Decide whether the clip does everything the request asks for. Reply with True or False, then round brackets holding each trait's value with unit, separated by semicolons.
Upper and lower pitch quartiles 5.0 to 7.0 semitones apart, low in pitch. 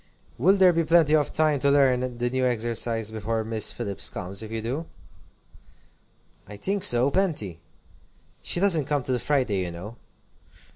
True (5.4 semitones; 125 Hz)